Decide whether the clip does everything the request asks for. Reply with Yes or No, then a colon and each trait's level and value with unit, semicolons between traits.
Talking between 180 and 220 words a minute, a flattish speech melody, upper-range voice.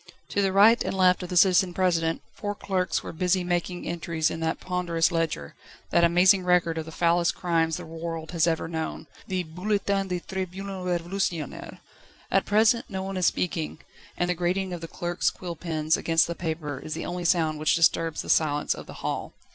No: average, 200 wpm; narrow, 2.2 semitones; medium, 175 Hz